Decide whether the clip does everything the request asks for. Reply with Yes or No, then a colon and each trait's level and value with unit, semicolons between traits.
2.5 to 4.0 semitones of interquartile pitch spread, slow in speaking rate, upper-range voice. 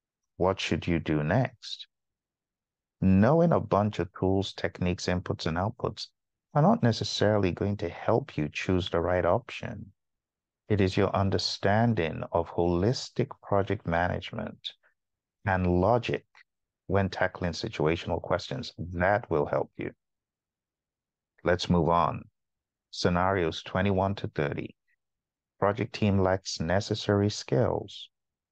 No: average, 2.9 semitones; slow, 115 wpm; very low, 95 Hz